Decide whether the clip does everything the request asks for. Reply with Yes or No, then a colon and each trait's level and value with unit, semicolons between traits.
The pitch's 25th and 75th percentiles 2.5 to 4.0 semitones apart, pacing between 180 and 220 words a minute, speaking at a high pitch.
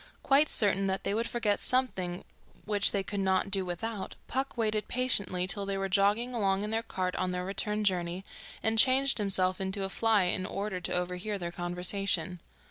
Yes: average, 2.8 semitones; average, 190 wpm; high, 195 Hz